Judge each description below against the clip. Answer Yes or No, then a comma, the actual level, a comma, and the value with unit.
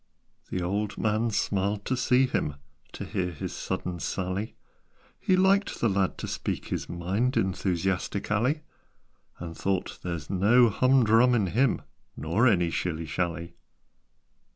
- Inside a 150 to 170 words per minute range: No, slow, 135 wpm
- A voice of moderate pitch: No, low, 100 Hz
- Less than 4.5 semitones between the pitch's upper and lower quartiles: No, average, 4.9 semitones